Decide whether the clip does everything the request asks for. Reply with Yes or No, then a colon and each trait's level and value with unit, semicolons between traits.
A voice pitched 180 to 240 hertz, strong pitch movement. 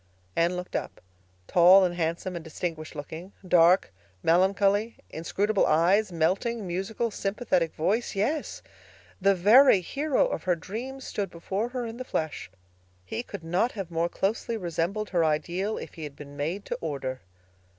No: medium, 185 Hz; average, 4.3 semitones